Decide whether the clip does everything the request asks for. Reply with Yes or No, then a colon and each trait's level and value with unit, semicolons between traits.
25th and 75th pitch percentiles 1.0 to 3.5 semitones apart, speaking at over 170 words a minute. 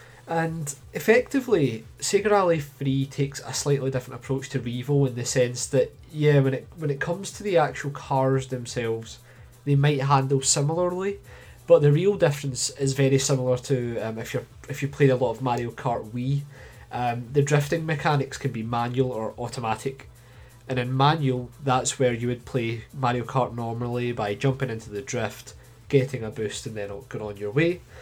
Yes: average, 2.8 semitones; average, 180 wpm